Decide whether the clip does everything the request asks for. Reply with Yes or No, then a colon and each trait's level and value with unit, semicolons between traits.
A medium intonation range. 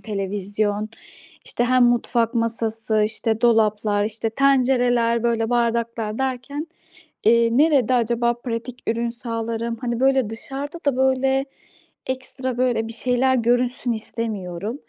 No: narrow, 2.2 semitones